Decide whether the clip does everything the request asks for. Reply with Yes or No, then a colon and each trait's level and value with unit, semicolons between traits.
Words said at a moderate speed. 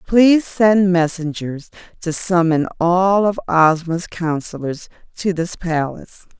No: slow, 115 wpm